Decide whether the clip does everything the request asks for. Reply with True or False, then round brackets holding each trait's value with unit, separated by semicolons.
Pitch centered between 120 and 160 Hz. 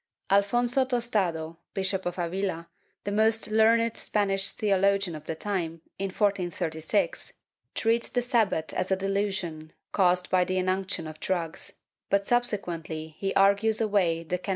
False (195 Hz)